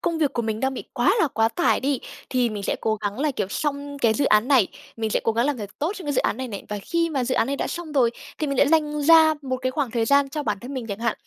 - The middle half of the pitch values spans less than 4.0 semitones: No, average, 4.5 semitones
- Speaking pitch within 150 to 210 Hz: No, very high, 265 Hz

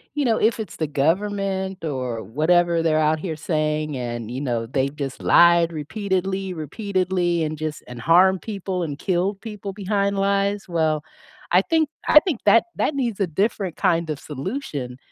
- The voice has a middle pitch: Yes, medium, 175 Hz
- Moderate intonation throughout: Yes, average, 4.6 semitones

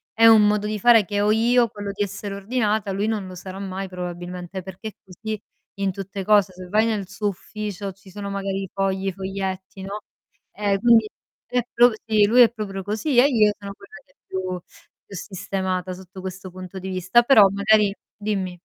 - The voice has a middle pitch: No, high, 200 Hz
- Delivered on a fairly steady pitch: Yes, narrow, 2.1 semitones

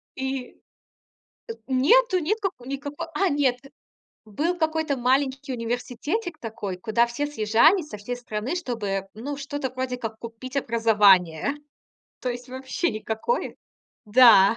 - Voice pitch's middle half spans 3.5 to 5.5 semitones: Yes, average, 4.4 semitones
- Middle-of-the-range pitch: No, very high, 255 Hz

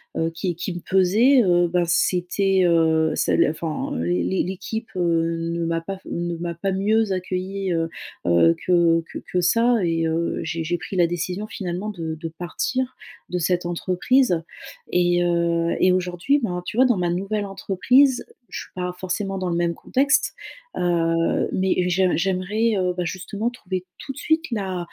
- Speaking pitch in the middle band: Yes, medium, 180 Hz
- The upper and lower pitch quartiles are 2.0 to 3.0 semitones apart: Yes, narrow, 2.5 semitones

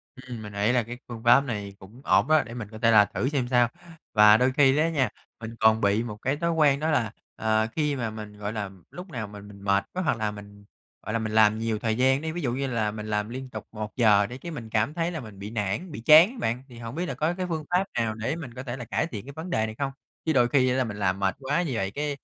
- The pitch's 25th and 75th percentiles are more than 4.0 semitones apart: Yes, average, 4.8 semitones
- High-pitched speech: No, low, 120 Hz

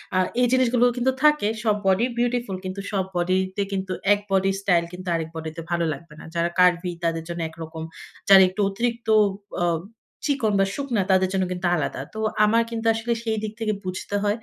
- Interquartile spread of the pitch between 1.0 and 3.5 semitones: No, average, 4.5 semitones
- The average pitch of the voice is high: Yes, high, 195 Hz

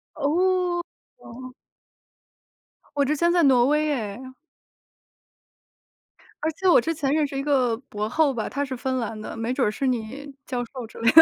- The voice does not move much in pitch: No, average, 3.8 semitones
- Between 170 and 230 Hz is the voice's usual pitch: No, very high, 270 Hz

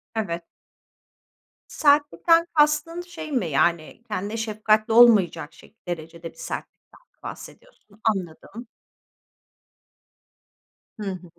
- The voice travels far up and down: Yes, wide, 8.7 semitones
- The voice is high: Yes, high, 215 Hz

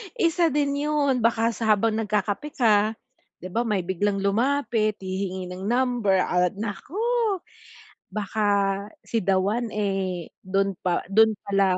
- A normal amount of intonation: Yes, average, 3.9 semitones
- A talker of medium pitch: No, high, 210 Hz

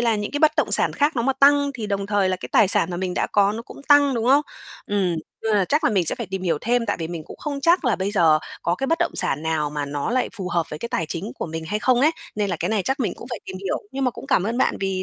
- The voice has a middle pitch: No, high, 205 Hz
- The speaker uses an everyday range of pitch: No, wide, 6.1 semitones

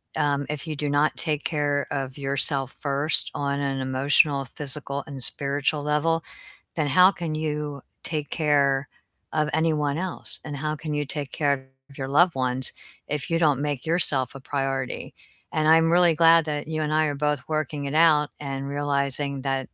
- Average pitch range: No, narrow, 1.9 semitones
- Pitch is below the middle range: No, medium, 145 Hz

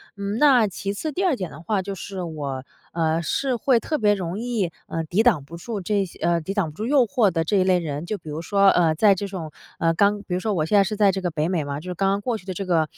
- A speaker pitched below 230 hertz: Yes, high, 190 Hz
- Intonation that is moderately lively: Yes, average, 4.0 semitones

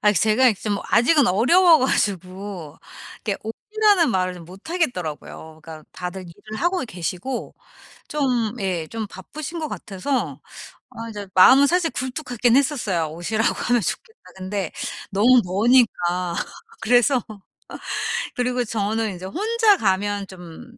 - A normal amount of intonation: No, wide, 6.0 semitones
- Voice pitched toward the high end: Yes, high, 215 Hz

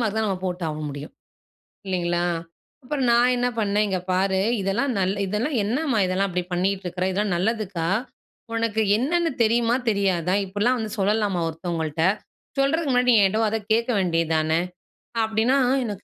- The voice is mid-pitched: No, high, 200 Hz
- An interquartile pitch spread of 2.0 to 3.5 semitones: No, average, 4.2 semitones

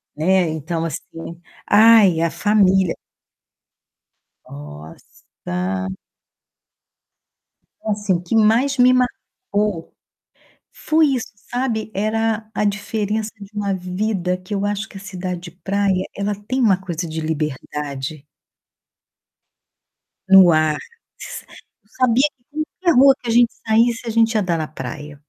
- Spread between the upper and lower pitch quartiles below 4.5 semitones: No, average, 5.1 semitones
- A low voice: No, high, 195 Hz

